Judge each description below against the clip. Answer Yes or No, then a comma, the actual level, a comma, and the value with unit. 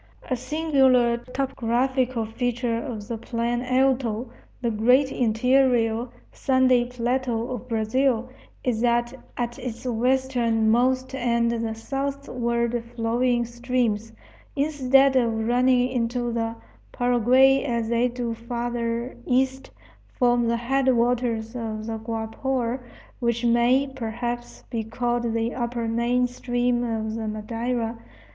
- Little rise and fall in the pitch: Yes, narrow, 1.7 semitones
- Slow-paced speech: Yes, slow, 115 wpm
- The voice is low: No, high, 240 Hz